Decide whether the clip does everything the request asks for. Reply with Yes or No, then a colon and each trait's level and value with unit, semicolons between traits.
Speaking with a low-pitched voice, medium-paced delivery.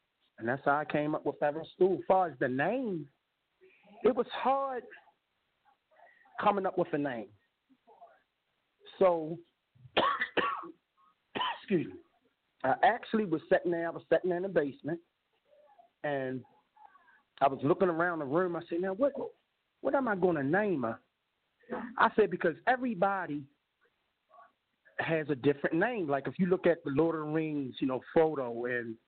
No: medium, 170 Hz; average, 155 wpm